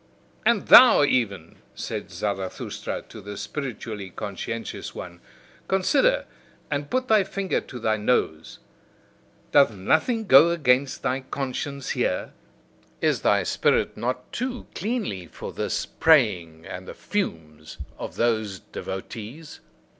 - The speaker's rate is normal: No, slow, 120 wpm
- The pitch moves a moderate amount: No, wide, 8.9 semitones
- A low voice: Yes, low, 125 Hz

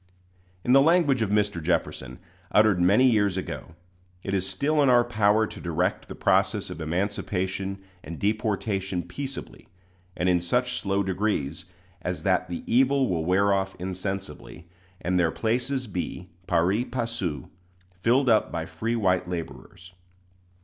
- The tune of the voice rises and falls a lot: No, average, 4.5 semitones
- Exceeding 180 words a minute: No, average, 145 wpm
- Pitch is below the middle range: Yes, low, 100 Hz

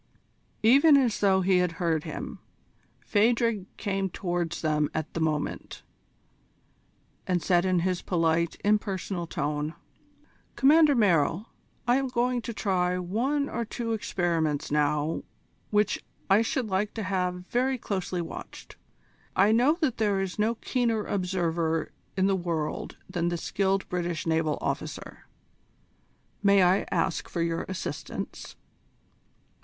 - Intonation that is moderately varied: Yes, average, 4.6 semitones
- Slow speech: Yes, slow, 130 wpm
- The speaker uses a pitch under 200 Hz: Yes, high, 190 Hz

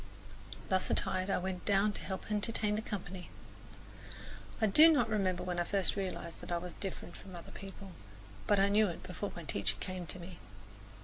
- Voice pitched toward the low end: No, high, 190 Hz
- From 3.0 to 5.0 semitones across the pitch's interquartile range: No, narrow, 2.4 semitones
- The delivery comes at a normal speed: Yes, average, 190 wpm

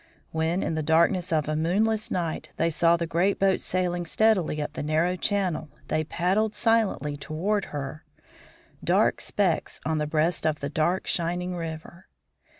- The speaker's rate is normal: Yes, average, 160 wpm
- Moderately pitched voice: Yes, medium, 170 Hz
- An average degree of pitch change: Yes, average, 3.0 semitones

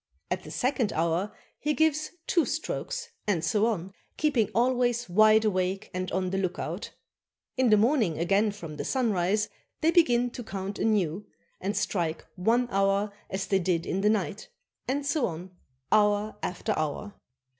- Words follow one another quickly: No, average, 160 wpm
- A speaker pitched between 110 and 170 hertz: No, high, 210 Hz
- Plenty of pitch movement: No, average, 4.6 semitones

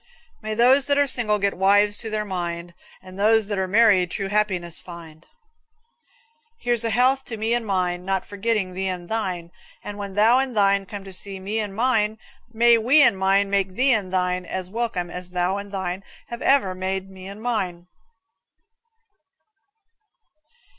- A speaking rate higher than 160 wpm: Yes, average, 175 wpm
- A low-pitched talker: No, high, 200 Hz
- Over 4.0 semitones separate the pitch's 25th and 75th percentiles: No, average, 3.2 semitones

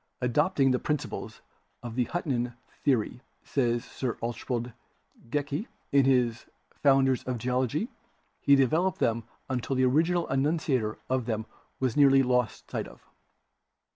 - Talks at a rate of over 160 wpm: No, average, 140 wpm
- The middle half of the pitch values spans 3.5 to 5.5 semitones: No, average, 2.7 semitones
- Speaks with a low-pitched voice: Yes, low, 130 Hz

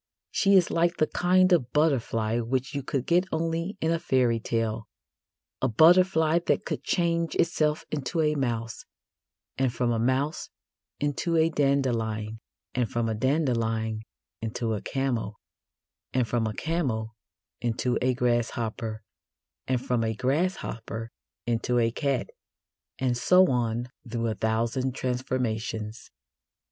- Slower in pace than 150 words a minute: Yes, slow, 135 wpm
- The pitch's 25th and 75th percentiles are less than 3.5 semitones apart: No, average, 5.3 semitones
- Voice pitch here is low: Yes, low, 125 Hz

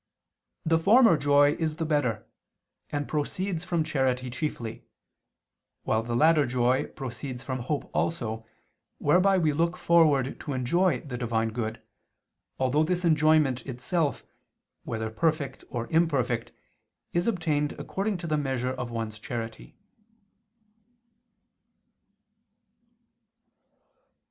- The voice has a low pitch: No, medium, 145 Hz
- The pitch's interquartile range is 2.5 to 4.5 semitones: No, average, 4.9 semitones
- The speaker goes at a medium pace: No, slow, 110 wpm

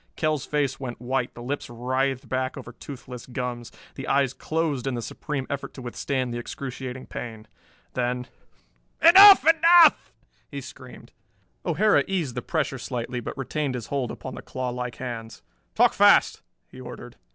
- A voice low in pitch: Yes, low, 130 Hz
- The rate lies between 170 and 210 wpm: No, average, 155 wpm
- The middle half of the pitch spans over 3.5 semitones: No, narrow, 2.5 semitones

